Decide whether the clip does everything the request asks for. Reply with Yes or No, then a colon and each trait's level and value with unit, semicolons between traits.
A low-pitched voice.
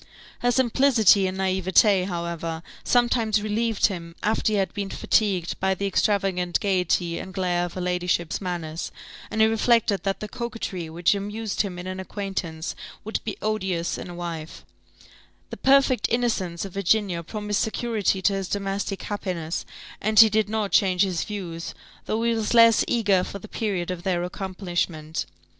No: high, 195 Hz